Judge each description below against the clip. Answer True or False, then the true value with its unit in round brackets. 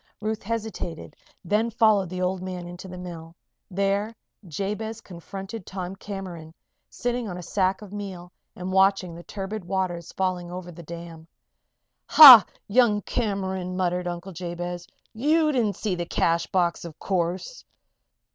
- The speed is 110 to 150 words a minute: True (145 wpm)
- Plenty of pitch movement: False (3.0 semitones)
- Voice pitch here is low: False (185 Hz)